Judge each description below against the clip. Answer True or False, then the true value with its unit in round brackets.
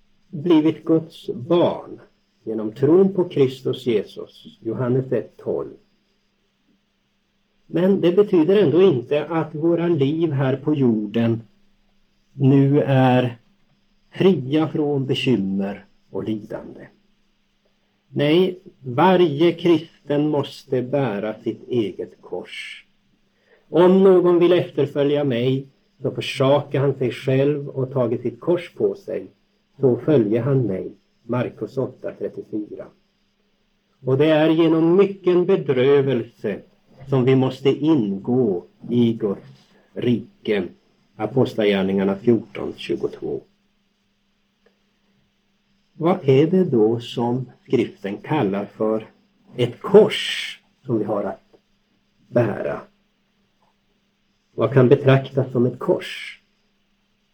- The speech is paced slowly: True (100 wpm)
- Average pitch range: False (6.4 semitones)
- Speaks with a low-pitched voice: False (145 Hz)